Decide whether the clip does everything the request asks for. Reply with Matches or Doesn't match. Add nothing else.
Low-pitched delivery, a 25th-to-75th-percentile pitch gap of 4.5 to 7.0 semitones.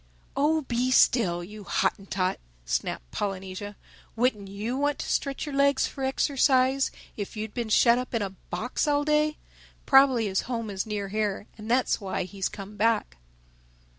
Doesn't match